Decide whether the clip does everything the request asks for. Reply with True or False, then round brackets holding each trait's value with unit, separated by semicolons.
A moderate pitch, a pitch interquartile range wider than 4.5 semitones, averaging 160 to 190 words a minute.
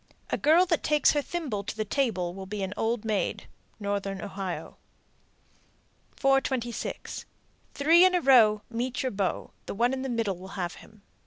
False (225 Hz; 5.4 semitones; 170 wpm)